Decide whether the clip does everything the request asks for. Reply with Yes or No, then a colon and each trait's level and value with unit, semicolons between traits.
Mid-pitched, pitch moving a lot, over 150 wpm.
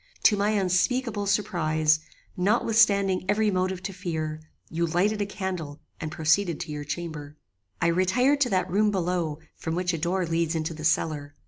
No: medium, 180 Hz; average, 4.0 semitones; average, 165 wpm